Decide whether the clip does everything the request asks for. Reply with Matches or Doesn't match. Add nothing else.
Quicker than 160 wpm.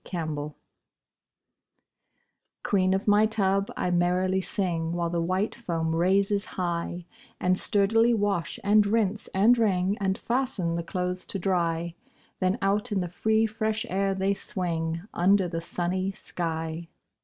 Doesn't match